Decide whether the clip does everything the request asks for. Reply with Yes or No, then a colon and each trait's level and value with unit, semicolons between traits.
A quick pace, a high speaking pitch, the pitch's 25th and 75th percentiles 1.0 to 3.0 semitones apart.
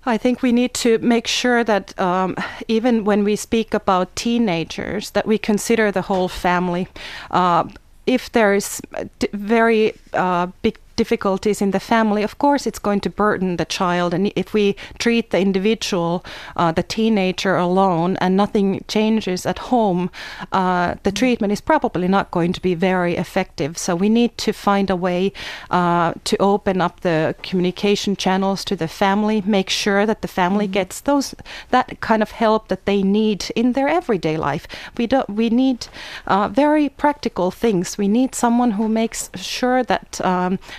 No: fast, 170 wpm; high, 205 Hz; average, 3.7 semitones